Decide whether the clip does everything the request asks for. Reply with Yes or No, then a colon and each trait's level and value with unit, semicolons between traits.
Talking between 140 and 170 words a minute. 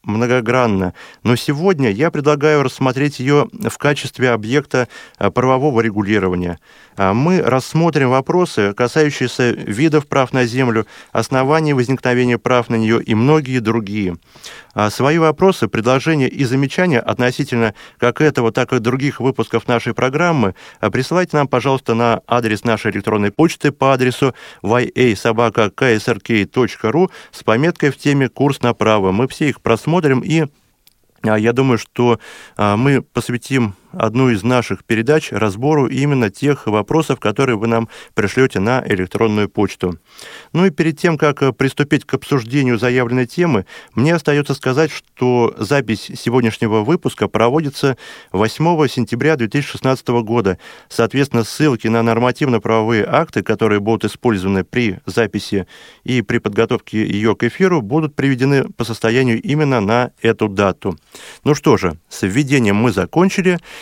No: average, 130 wpm